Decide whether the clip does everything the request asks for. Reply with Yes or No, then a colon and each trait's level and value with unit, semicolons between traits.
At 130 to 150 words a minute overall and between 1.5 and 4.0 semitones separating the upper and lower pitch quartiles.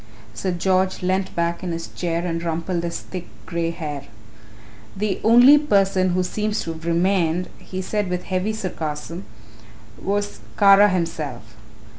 Yes: average, 145 wpm; average, 2.8 semitones